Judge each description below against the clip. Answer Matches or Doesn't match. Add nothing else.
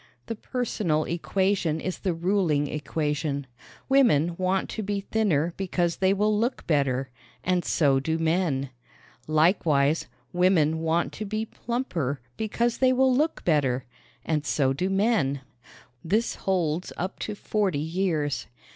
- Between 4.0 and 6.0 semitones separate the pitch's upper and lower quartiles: Matches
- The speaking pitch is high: Doesn't match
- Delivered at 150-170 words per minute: Doesn't match